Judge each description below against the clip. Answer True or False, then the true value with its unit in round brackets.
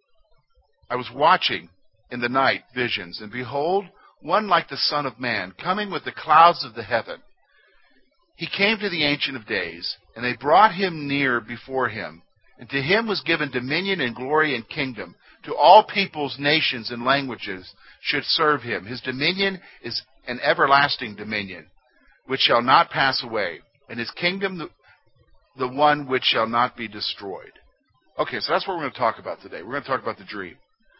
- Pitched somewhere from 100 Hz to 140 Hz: True (135 Hz)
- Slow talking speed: False (180 wpm)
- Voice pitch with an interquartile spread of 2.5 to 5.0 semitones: False (5.5 semitones)